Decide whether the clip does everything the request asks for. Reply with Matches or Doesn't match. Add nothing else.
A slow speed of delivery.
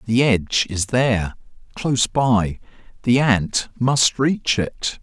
Matches